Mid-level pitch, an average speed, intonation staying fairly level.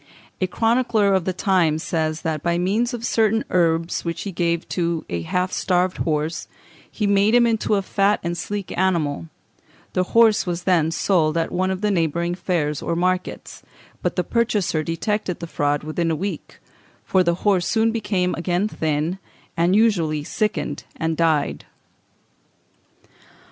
No: medium, 180 Hz; average, 160 wpm; average, 3.6 semitones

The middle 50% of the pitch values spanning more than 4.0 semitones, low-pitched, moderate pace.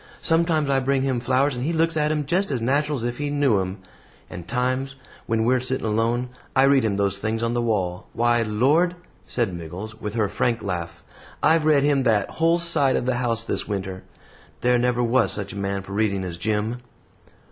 No: average, 4.7 semitones; low, 120 Hz; fast, 210 wpm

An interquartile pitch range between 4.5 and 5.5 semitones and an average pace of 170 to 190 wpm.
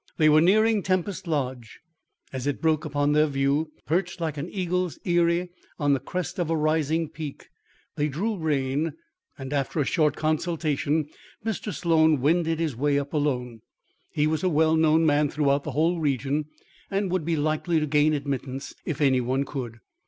No: average, 2.7 semitones; average, 175 wpm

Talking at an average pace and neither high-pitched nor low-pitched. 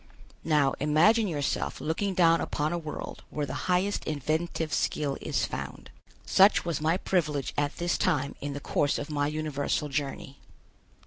Yes: average, 155 wpm; medium, 155 Hz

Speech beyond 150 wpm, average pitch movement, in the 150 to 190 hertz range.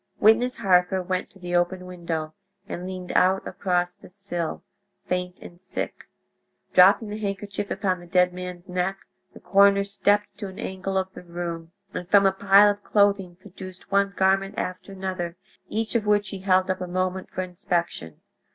No: average, 175 wpm; narrow, 1.8 semitones; medium, 185 Hz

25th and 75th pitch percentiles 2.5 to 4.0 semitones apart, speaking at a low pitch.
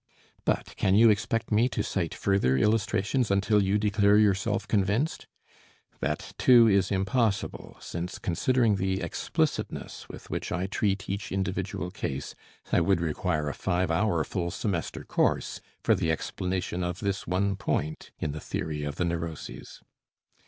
Yes: average, 3.2 semitones; very low, 95 Hz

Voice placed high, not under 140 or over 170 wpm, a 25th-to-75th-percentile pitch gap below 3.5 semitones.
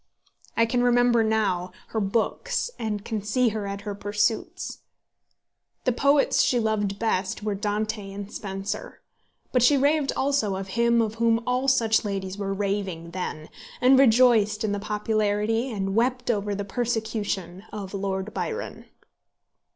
Yes: high, 215 Hz; average, 150 wpm; average, 2.9 semitones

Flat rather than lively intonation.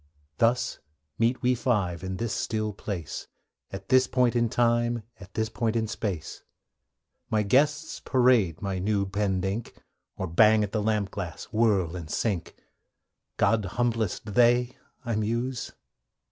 No: average, 3.4 semitones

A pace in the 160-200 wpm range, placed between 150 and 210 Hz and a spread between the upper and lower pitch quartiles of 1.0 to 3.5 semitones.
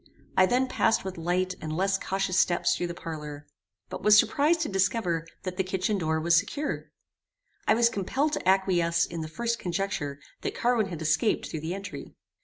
No: average, 190 wpm; medium, 185 Hz; average, 4.1 semitones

